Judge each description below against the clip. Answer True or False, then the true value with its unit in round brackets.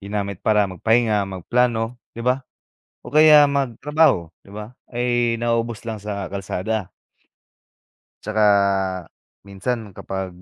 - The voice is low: True (110 Hz)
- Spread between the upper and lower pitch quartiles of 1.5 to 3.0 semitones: False (3.4 semitones)